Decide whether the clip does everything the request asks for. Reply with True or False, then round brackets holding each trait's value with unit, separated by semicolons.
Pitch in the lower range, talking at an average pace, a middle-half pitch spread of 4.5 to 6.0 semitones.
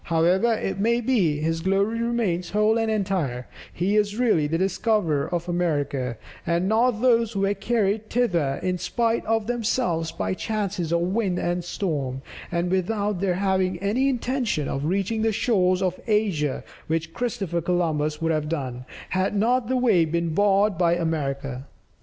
False (185 Hz; 160 wpm; 4.9 semitones)